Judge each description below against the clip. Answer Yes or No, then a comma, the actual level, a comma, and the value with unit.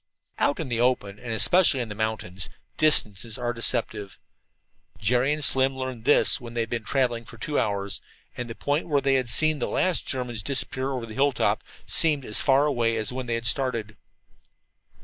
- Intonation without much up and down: No, average, 3.2 semitones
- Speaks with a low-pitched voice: Yes, low, 125 Hz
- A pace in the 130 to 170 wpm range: No, average, 190 wpm